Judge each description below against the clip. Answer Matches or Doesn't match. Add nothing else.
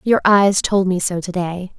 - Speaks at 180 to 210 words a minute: Matches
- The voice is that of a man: Doesn't match